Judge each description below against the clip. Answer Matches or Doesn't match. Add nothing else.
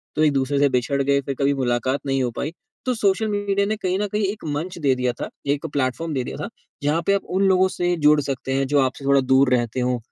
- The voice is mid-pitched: Matches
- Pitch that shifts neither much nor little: Doesn't match